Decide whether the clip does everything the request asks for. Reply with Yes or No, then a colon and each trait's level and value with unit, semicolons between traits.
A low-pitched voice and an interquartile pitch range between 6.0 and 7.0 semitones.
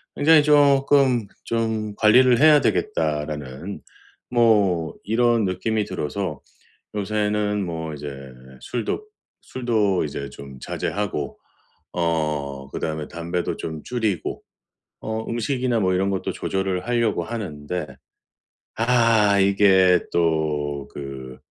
Yes: low, 100 Hz; wide, 6.6 semitones